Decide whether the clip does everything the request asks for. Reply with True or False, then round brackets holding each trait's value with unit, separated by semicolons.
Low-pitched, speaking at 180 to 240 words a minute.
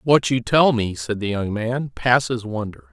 True (120 Hz; 205 wpm)